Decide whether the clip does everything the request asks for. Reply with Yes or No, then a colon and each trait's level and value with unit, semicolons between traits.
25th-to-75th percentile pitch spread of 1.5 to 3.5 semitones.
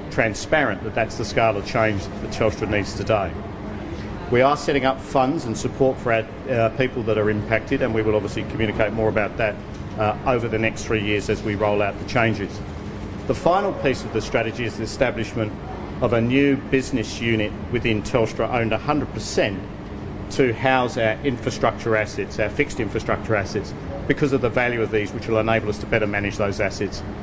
Yes: narrow, 2.5 semitones